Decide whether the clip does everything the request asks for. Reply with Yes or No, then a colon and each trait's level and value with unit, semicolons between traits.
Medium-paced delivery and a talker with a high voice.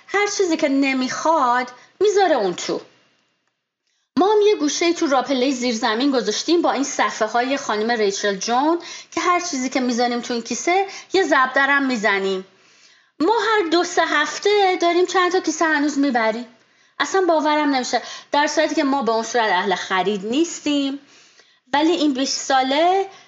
No: fast, 160 wpm; very high, 280 Hz